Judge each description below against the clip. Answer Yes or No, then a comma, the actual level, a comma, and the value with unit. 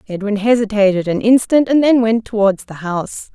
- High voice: Yes, high, 215 Hz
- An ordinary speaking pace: Yes, average, 180 wpm